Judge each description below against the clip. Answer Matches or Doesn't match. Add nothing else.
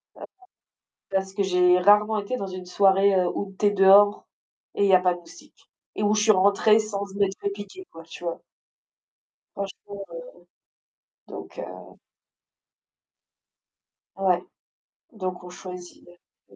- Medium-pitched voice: Doesn't match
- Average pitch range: Doesn't match